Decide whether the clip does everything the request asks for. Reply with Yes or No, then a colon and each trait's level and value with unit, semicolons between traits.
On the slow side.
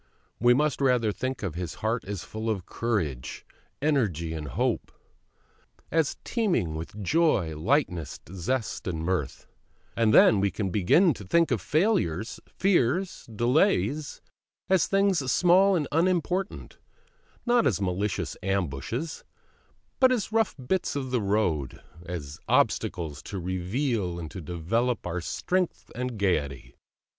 Yes: slow, 130 wpm